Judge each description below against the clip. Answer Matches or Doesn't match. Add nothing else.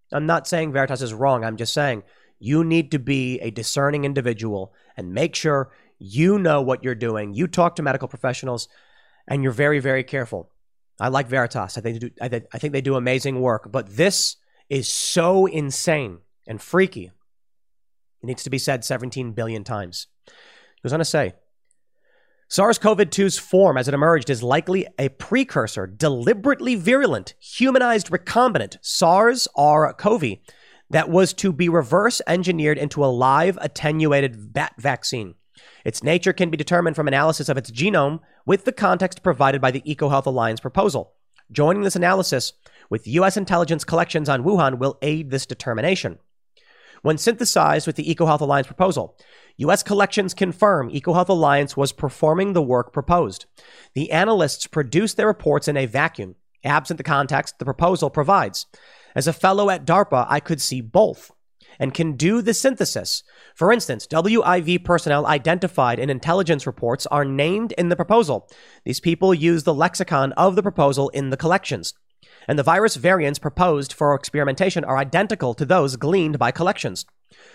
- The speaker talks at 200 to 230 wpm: Doesn't match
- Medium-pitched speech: Matches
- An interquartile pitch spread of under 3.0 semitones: Doesn't match